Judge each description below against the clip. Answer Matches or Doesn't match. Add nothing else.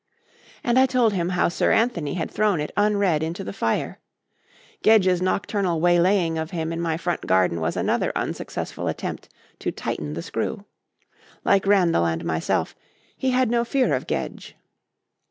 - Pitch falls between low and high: Matches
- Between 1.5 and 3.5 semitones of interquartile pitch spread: Doesn't match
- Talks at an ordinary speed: Matches